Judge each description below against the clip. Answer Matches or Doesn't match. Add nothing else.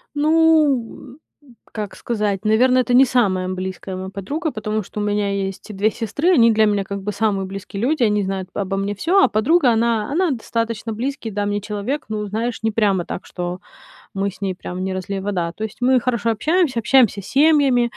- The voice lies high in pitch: Matches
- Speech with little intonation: Doesn't match